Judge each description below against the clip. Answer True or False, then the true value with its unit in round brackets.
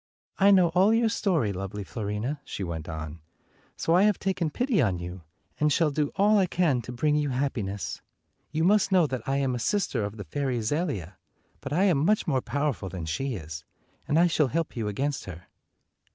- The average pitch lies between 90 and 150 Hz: True (140 Hz)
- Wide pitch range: True (8.9 semitones)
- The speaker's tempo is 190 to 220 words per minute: True (205 wpm)